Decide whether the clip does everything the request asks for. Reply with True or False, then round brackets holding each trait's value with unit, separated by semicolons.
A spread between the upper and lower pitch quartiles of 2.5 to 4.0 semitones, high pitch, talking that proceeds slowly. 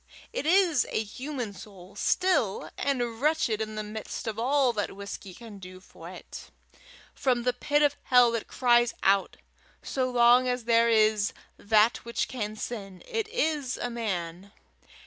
False (3.6 semitones; 235 Hz; 160 wpm)